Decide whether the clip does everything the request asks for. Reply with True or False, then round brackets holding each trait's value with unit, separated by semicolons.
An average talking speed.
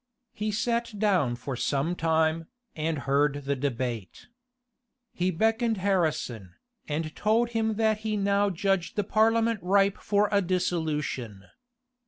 False (130 wpm)